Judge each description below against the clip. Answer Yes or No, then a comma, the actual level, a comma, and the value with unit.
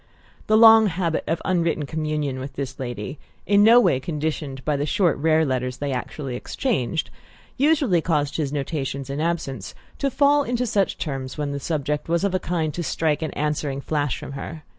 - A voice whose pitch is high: No, medium, 155 Hz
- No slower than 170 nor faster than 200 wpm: Yes, average, 185 wpm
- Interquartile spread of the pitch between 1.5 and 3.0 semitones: No, average, 4.2 semitones